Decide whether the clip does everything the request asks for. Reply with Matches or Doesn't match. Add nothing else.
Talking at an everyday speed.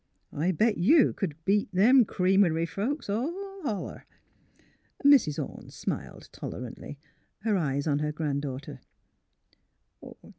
Doesn't match